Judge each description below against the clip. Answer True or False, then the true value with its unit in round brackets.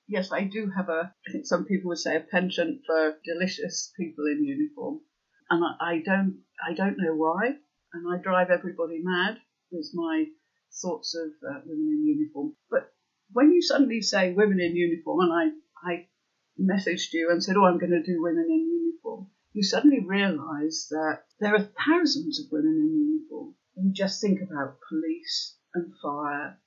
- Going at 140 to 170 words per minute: False (180 wpm)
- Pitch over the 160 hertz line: True (190 Hz)